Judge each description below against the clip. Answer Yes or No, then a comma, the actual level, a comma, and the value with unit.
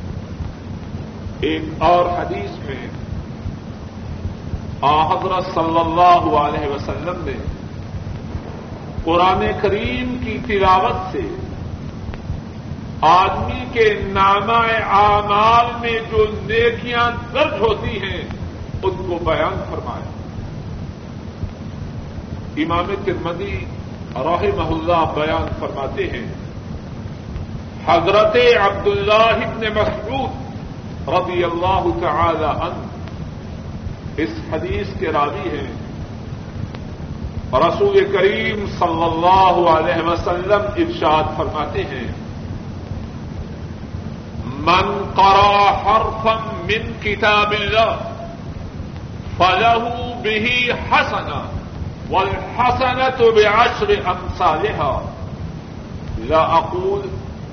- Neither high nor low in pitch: Yes, medium, 180 Hz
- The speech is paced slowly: Yes, slow, 75 wpm